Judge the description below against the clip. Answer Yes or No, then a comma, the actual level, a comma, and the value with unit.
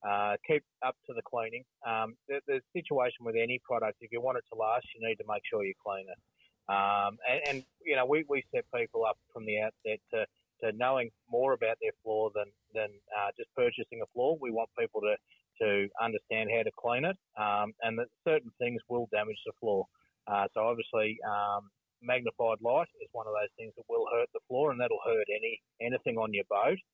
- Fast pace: Yes, fast, 215 wpm